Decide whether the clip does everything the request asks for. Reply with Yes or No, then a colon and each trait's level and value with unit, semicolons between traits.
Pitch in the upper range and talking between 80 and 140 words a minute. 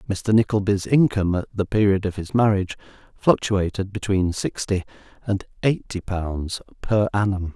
No: low, 100 Hz; slow, 135 wpm